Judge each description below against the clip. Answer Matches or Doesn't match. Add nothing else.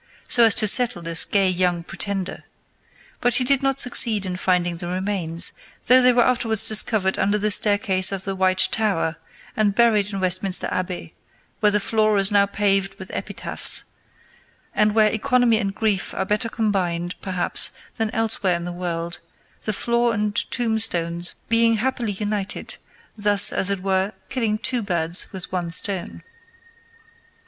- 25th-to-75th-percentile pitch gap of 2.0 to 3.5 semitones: Matches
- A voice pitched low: Doesn't match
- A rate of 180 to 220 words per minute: Doesn't match